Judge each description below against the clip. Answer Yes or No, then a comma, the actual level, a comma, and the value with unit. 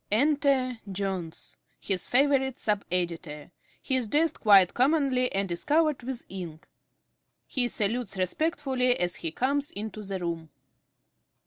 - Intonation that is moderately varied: No, wide, 6.5 semitones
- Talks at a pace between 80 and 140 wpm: Yes, slow, 135 wpm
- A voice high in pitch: Yes, high, 225 Hz